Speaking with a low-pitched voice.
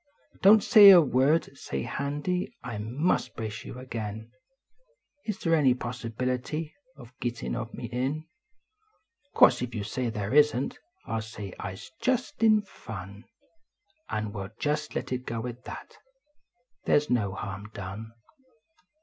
Yes: low, 125 Hz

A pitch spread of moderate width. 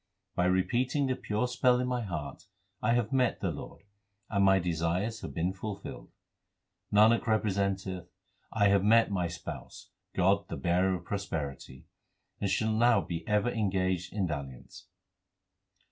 Yes: average, 3.6 semitones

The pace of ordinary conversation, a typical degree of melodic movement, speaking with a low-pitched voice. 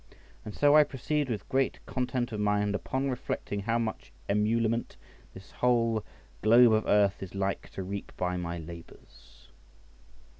Yes: average, 150 wpm; average, 3.8 semitones; low, 110 Hz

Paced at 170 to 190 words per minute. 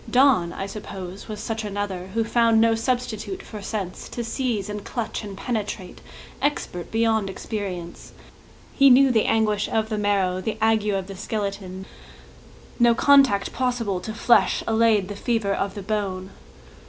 No: average, 155 wpm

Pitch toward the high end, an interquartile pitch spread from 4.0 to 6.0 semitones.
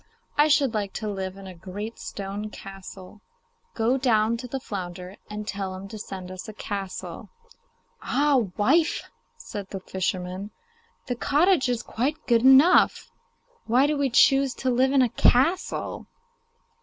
Yes: high, 220 Hz; wide, 5.4 semitones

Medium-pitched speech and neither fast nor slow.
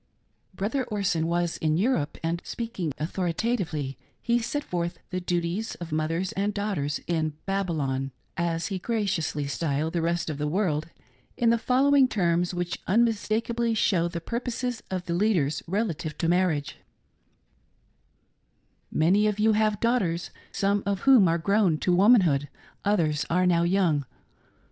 Yes: medium, 180 Hz; average, 150 wpm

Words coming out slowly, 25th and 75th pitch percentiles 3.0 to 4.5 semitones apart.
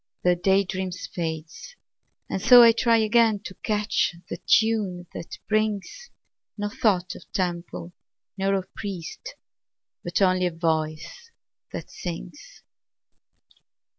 Yes: slow, 125 wpm; average, 3.7 semitones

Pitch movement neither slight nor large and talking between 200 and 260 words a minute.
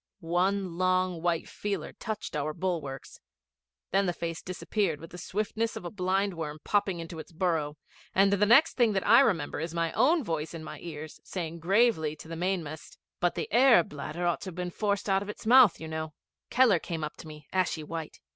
Yes: average, 3.8 semitones; fast, 205 wpm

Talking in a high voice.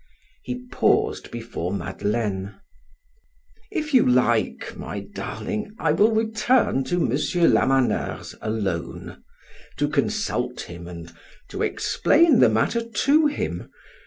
No: medium, 145 Hz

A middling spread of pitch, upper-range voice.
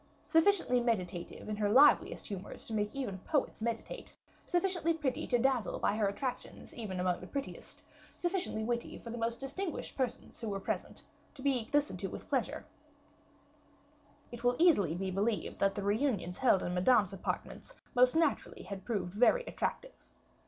No: wide, 5.8 semitones; high, 235 Hz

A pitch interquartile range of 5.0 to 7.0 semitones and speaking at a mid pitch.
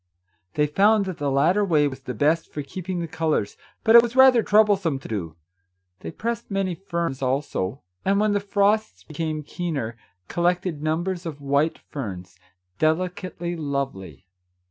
Yes: wide, 5.6 semitones; medium, 165 Hz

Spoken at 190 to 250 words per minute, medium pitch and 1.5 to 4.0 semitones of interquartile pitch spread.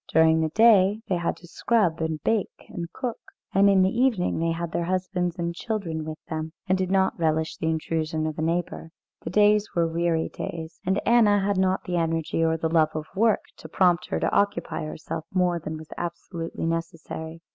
Yes: average, 200 wpm; medium, 170 Hz; average, 2.9 semitones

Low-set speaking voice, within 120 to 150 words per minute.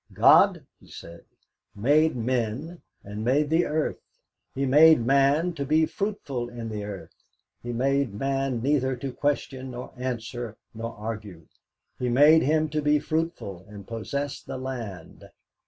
Yes: low, 130 Hz; average, 145 wpm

